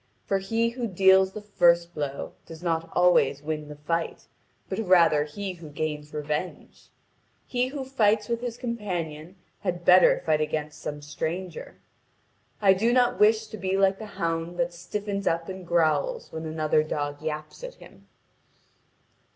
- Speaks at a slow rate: No, average, 160 wpm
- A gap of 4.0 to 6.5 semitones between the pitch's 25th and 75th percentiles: Yes, average, 4.8 semitones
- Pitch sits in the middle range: Yes, medium, 175 Hz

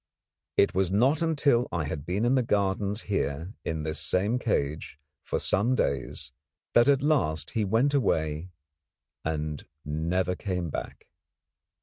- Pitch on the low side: Yes, very low, 95 Hz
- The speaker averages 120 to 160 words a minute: Yes, average, 140 wpm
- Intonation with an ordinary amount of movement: No, wide, 7.2 semitones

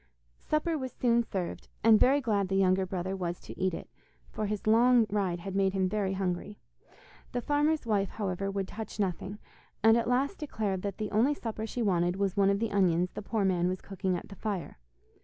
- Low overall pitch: No, high, 200 Hz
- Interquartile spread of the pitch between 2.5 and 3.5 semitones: Yes, average, 3.2 semitones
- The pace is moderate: No, fast, 210 wpm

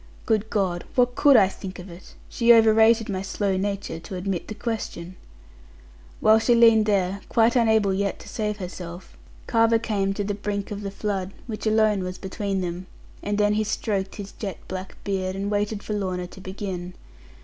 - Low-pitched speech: No, high, 200 Hz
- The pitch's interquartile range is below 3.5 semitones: Yes, narrow, 2.5 semitones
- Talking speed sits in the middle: Yes, average, 190 wpm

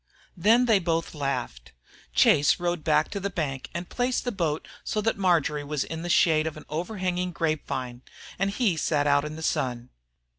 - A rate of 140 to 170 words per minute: No, average, 190 wpm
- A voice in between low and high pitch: Yes, medium, 165 Hz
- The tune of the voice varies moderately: Yes, average, 4.0 semitones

